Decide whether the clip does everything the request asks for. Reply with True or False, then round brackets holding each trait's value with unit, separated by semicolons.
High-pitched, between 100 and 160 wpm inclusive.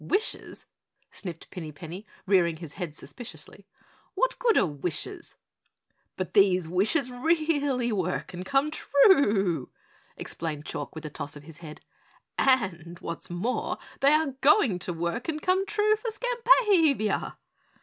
True (210 Hz; 140 wpm)